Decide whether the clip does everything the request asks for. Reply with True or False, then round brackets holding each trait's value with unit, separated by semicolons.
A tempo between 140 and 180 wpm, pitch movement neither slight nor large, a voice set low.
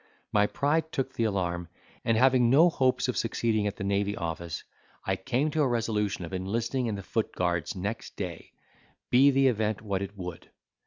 False (190 wpm; 4.8 semitones; 110 Hz)